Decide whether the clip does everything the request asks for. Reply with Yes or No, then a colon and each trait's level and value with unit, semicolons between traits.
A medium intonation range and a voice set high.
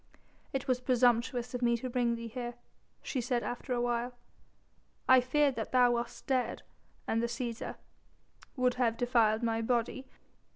No: narrow, 1.3 semitones; high, 245 Hz